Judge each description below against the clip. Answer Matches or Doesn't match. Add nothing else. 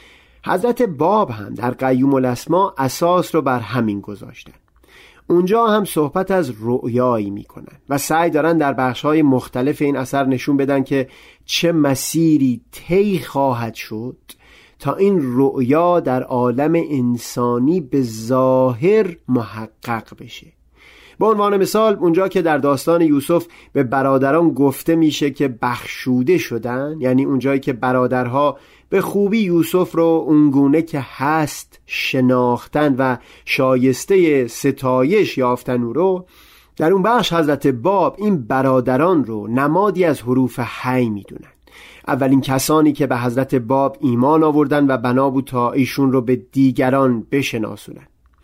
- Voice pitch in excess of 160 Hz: Doesn't match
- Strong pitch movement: Doesn't match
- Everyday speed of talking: Matches